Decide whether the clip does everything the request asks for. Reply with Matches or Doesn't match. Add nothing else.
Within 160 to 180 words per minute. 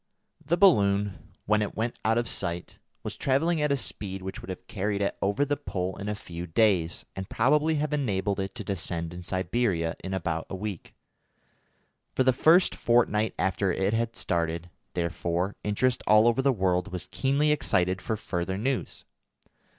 Matches